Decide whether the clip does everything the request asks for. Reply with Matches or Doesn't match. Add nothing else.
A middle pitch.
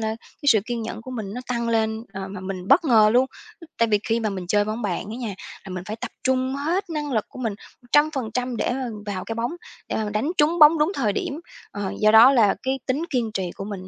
Doesn't match